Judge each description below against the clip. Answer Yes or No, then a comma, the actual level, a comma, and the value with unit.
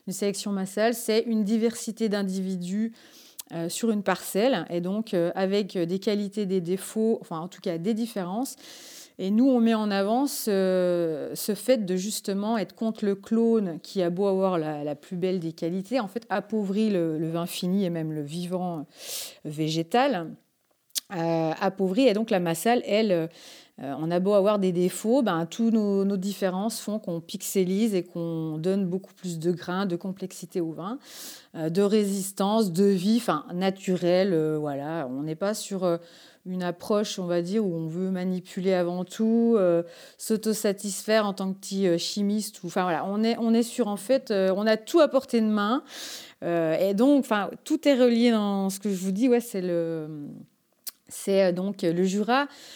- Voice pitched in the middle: No, high, 195 Hz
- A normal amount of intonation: Yes, average, 3.7 semitones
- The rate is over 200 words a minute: No, average, 190 wpm